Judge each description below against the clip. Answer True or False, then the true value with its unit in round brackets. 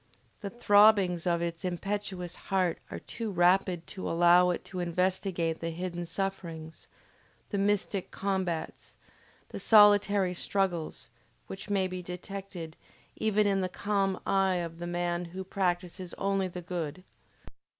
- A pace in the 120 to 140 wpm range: True (135 wpm)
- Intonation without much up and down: True (2.1 semitones)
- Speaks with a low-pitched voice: False (185 Hz)